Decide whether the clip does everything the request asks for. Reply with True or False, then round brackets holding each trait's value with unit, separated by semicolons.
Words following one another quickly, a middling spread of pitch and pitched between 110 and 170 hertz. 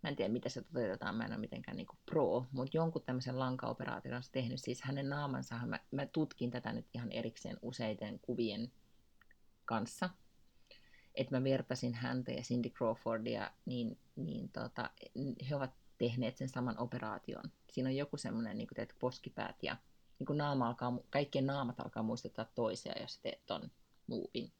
False (170 wpm; 2.1 semitones; 125 Hz)